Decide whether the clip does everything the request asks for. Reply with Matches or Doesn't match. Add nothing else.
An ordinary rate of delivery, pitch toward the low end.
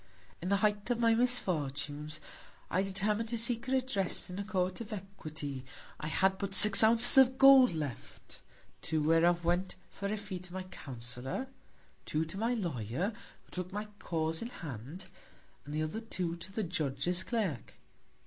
Doesn't match